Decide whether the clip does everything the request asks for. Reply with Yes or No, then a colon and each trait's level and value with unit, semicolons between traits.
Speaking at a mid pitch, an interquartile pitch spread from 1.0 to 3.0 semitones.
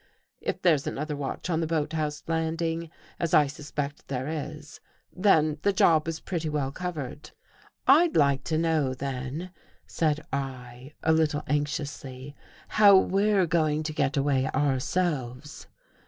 Yes: medium, 150 Hz; average, 2.7 semitones